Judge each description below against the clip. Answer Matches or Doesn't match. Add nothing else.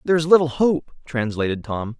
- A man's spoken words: Matches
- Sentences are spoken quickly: Doesn't match